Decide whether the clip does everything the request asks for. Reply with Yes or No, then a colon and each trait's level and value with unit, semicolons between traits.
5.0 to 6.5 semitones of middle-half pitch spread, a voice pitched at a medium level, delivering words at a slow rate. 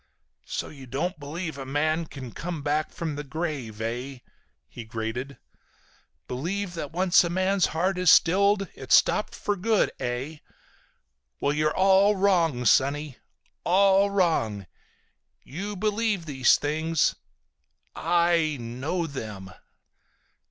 Yes: wide, 5.4 semitones; medium, 160 Hz; slow, 125 wpm